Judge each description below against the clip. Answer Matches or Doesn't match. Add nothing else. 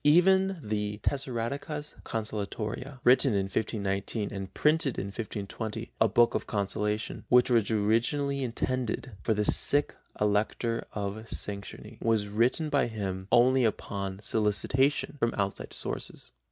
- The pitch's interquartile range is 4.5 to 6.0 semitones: Doesn't match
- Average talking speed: Doesn't match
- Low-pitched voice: Matches